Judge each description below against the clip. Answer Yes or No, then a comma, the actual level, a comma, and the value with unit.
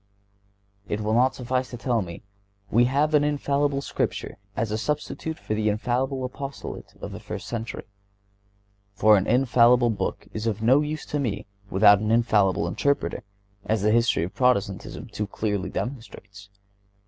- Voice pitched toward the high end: No, low, 115 Hz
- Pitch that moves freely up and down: No, average, 3.9 semitones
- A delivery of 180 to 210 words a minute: No, average, 160 wpm